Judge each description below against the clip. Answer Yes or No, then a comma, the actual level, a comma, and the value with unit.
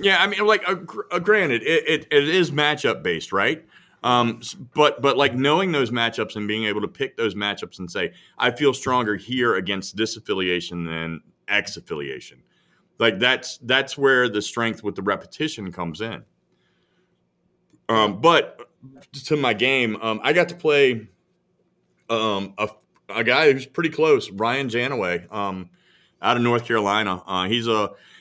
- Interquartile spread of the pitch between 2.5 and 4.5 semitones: No, wide, 5.4 semitones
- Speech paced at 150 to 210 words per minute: Yes, average, 165 wpm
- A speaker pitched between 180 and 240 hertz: No, low, 120 Hz